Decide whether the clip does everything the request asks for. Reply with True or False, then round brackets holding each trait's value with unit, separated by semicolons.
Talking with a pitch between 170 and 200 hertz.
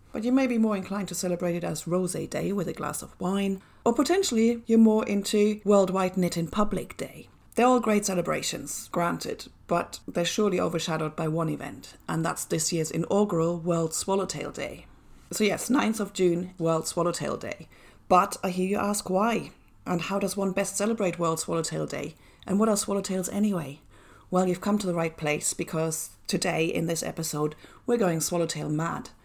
True (185 Hz)